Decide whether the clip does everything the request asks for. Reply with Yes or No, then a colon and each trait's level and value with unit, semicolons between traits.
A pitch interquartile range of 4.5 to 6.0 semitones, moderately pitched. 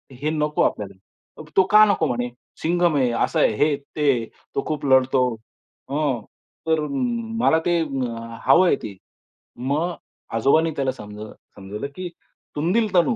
Yes: average, 5.2 semitones; medium, 145 Hz